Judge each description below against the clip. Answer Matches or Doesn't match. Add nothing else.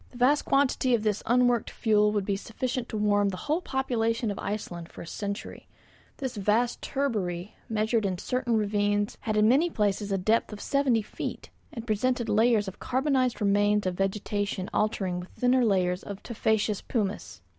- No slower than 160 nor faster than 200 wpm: Matches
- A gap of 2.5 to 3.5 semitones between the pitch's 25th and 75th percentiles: Matches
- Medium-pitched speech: Doesn't match